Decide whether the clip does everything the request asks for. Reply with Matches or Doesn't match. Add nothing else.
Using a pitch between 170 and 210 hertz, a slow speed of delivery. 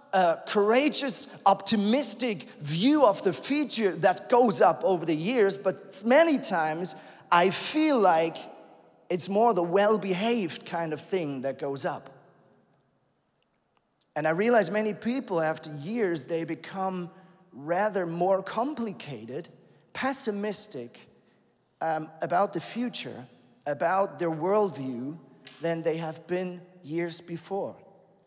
Matches